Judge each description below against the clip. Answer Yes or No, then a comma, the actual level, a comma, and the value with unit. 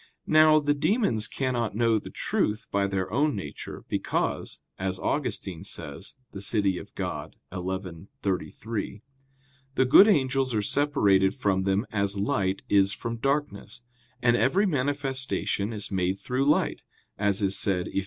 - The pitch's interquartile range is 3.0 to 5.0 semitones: No, wide, 5.6 semitones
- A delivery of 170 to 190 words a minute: No, average, 145 wpm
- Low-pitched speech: Yes, low, 105 Hz